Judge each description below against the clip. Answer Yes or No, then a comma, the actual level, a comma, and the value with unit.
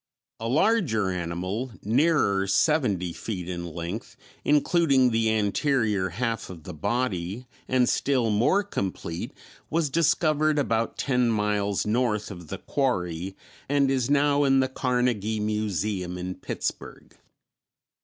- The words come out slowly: Yes, slow, 125 wpm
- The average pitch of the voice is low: Yes, low, 110 Hz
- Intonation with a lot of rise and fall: Yes, wide, 5.8 semitones